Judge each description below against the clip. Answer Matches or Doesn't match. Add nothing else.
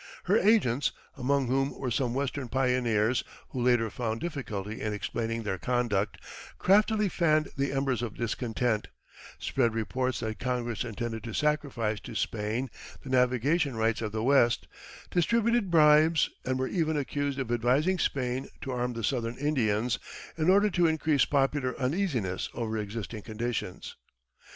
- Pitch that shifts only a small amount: Doesn't match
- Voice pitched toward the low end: Matches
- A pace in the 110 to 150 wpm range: Matches